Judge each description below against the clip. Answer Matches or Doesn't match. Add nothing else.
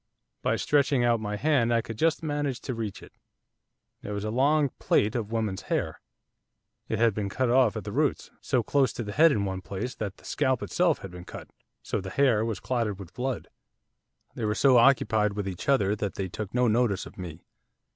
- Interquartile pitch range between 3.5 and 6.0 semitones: Matches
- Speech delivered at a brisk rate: Matches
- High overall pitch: Doesn't match